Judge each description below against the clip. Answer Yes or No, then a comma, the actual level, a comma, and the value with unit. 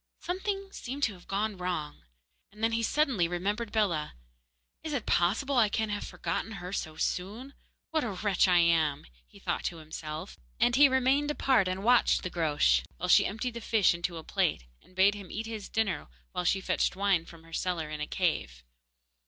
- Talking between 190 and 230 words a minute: Yes, average, 195 wpm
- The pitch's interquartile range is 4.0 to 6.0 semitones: Yes, average, 5.2 semitones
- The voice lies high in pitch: Yes, high, 195 Hz